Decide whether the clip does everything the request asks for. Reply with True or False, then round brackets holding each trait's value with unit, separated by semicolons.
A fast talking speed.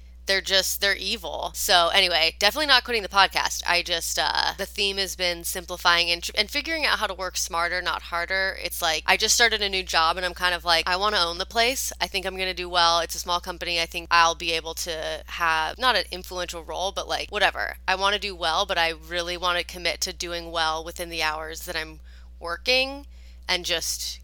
True (240 wpm)